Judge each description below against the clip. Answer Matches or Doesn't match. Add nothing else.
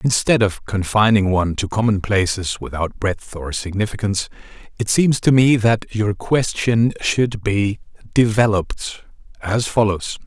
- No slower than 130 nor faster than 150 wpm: Matches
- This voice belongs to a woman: Doesn't match